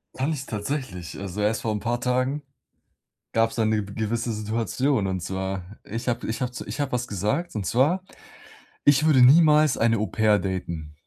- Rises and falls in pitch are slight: No, average, 4.2 semitones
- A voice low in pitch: Yes, low, 115 Hz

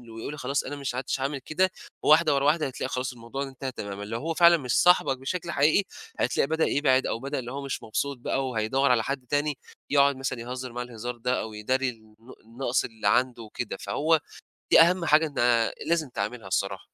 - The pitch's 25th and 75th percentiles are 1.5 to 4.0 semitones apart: Yes, average, 3.5 semitones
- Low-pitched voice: Yes, low, 130 Hz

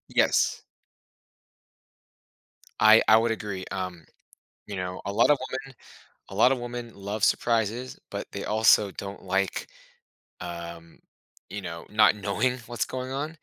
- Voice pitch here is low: Yes, low, 105 Hz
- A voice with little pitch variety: No, average, 3.9 semitones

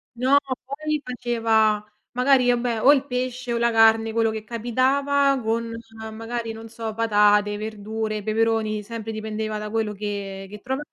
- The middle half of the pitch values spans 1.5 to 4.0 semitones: Yes, narrow, 2.5 semitones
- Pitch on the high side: Yes, high, 225 Hz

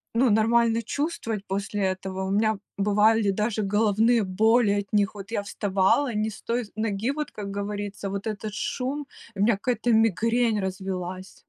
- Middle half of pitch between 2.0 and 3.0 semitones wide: Yes, narrow, 2.4 semitones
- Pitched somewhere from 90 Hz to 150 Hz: No, high, 210 Hz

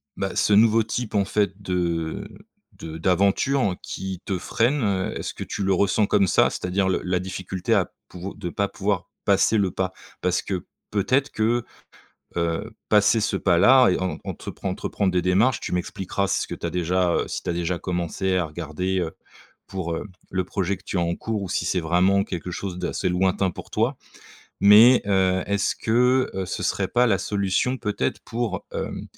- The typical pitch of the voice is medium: No, very low, 95 Hz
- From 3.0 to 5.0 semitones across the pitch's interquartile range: No, narrow, 2.4 semitones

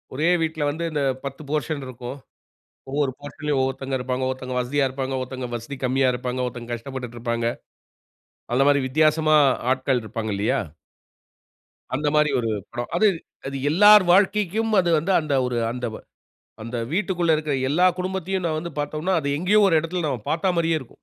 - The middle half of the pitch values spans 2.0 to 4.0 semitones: No, average, 4.4 semitones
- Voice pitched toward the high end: No, medium, 140 Hz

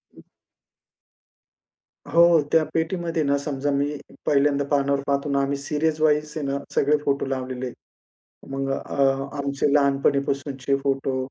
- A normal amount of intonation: No, narrow, 1.4 semitones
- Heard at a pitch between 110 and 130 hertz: No, medium, 140 Hz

